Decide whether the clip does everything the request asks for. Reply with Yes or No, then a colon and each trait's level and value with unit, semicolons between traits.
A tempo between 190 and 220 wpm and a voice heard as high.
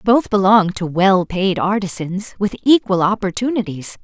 No: slow, 135 wpm; high, 195 Hz